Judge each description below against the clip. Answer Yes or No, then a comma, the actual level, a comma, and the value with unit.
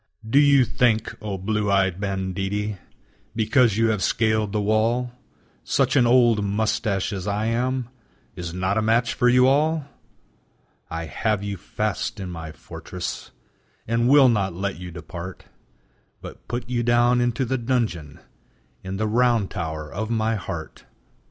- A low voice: Yes, low, 110 Hz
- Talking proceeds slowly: No, average, 150 wpm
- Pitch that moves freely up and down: No, average, 3.9 semitones